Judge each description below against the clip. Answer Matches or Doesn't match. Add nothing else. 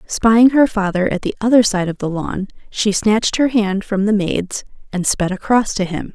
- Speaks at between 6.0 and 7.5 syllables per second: Doesn't match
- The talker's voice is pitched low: Doesn't match